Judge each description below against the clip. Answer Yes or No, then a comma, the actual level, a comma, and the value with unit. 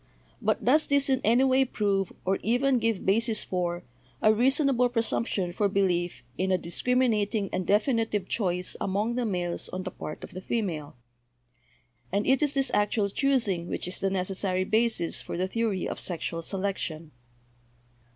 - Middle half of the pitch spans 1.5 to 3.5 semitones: No, average, 4.5 semitones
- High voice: Yes, high, 205 Hz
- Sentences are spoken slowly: No, average, 160 wpm